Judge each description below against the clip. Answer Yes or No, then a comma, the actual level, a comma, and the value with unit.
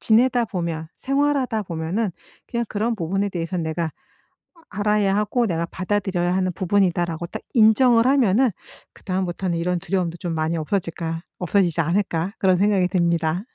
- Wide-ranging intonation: No, average, 3.7 semitones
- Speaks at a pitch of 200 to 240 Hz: No, medium, 185 Hz